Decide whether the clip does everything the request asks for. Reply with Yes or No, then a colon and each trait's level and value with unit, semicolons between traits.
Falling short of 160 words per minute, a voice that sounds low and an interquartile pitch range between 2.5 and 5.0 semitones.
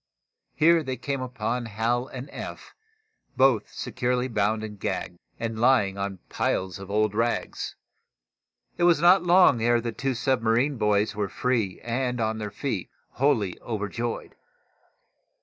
Yes: average, 140 wpm; low, 115 Hz; average, 3.7 semitones